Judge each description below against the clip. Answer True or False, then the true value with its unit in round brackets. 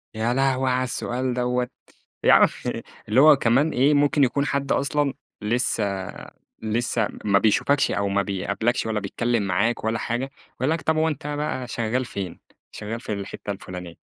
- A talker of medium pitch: False (120 Hz)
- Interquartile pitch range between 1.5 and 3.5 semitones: False (4.2 semitones)